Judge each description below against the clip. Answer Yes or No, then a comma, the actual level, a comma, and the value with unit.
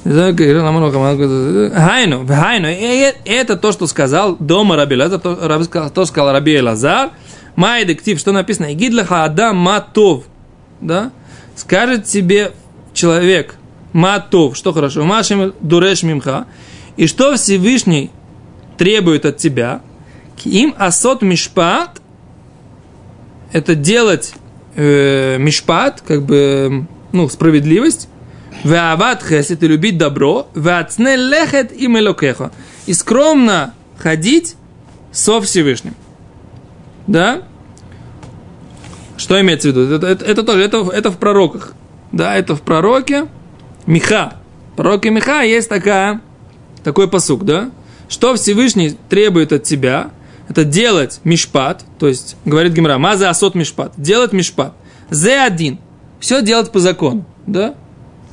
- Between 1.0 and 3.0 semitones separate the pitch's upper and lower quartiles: No, wide, 5.5 semitones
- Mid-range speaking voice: Yes, medium, 180 Hz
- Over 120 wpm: No, average, 115 wpm